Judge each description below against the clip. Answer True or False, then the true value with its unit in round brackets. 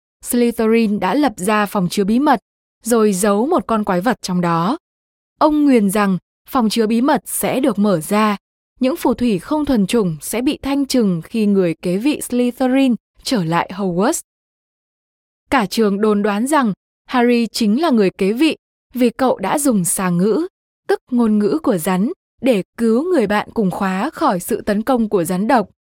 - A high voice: True (225 Hz)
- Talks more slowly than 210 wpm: True (185 wpm)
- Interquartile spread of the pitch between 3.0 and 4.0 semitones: False (4.6 semitones)